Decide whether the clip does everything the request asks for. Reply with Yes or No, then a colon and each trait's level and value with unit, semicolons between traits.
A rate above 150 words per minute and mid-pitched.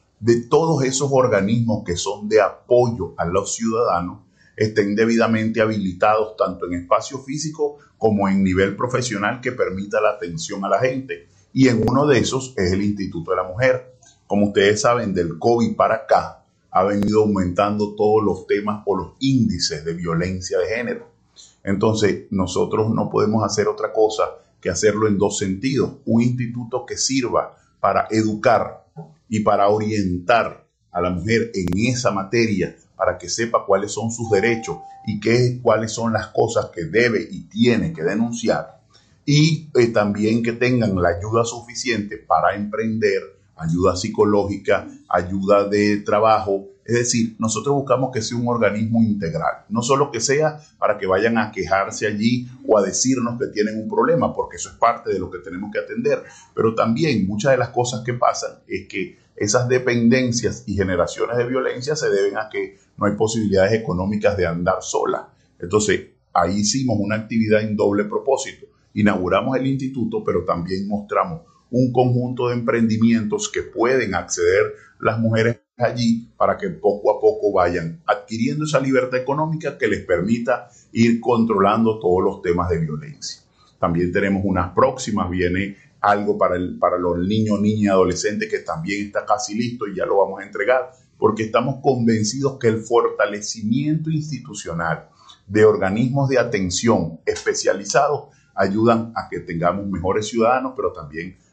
No: average, 160 wpm; low, 110 Hz